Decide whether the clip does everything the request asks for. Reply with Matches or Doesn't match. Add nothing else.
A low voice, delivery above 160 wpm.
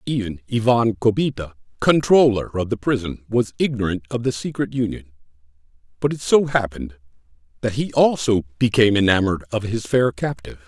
Doesn't match